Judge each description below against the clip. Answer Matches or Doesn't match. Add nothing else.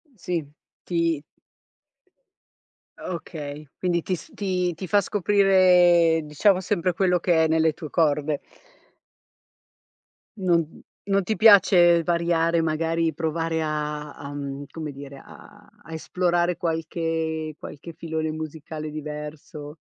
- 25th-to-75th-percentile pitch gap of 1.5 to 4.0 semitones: Matches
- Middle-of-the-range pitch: Matches